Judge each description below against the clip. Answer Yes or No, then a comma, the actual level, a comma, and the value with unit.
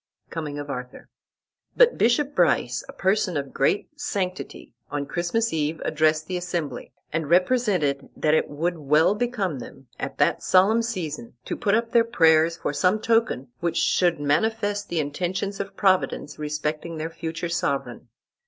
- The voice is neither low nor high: Yes, medium, 170 Hz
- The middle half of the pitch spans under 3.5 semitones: No, average, 5.3 semitones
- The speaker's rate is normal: Yes, average, 155 wpm